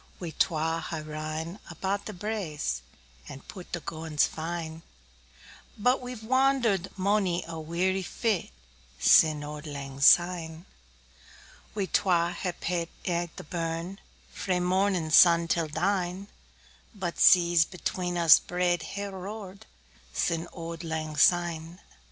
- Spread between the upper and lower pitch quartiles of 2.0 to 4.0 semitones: Yes, average, 2.8 semitones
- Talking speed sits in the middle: No, slow, 130 wpm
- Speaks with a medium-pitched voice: Yes, medium, 175 Hz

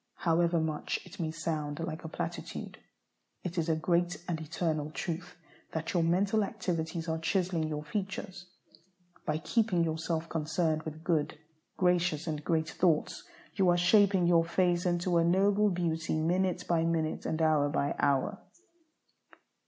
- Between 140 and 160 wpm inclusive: Yes, average, 150 wpm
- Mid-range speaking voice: Yes, medium, 165 Hz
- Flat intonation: Yes, narrow, 2.1 semitones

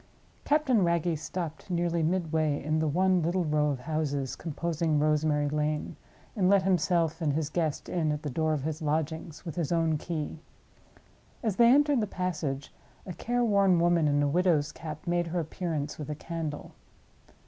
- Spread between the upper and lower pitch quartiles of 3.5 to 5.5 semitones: No, average, 2.8 semitones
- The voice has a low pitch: No, medium, 160 Hz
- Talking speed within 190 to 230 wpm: No, average, 175 wpm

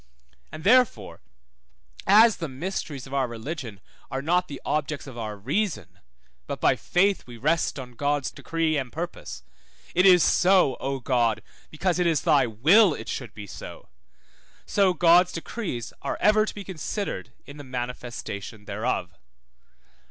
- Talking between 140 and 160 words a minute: Yes, average, 150 wpm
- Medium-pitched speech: Yes, medium, 145 Hz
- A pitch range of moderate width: No, wide, 6.7 semitones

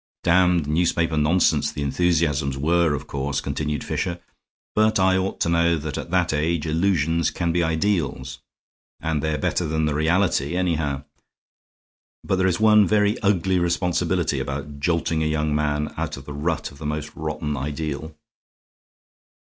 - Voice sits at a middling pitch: No, very low, 80 Hz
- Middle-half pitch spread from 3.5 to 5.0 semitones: No, average, 2.9 semitones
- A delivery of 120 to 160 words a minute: Yes, average, 155 wpm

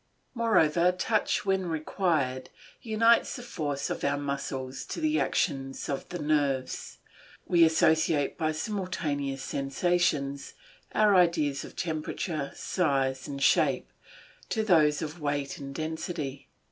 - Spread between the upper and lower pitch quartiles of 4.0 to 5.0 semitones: Yes, average, 4.4 semitones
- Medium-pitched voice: Yes, medium, 155 Hz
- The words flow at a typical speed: No, slow, 120 wpm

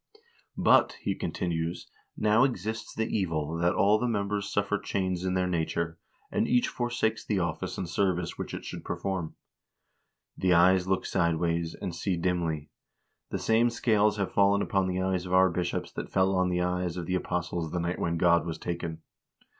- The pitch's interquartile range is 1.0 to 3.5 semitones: Yes, average, 2.8 semitones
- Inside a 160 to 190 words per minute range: Yes, average, 185 wpm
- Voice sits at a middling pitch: No, very low, 90 Hz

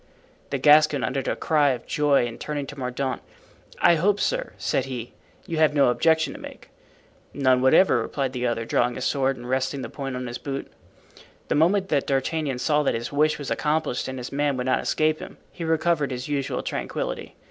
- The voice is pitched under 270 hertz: Yes, medium, 140 Hz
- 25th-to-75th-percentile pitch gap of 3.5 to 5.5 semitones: No, average, 3.0 semitones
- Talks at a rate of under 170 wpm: No, average, 200 wpm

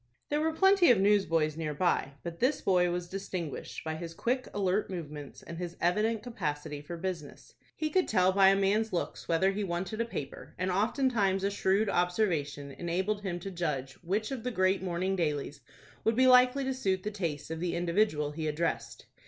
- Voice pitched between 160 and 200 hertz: Yes, medium, 185 Hz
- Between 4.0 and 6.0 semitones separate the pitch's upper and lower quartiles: Yes, average, 4.3 semitones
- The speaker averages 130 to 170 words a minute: No, average, 195 wpm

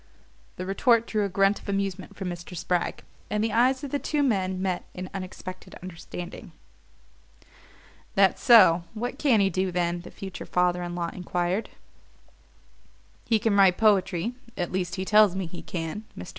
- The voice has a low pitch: No, high, 190 Hz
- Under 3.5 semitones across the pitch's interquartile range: Yes, average, 3.1 semitones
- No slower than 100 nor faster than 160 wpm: No, average, 170 wpm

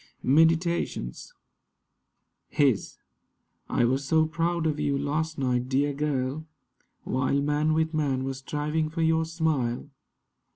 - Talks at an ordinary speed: No, slow, 120 wpm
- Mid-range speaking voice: Yes, medium, 150 Hz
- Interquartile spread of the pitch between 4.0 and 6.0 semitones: No, average, 3.1 semitones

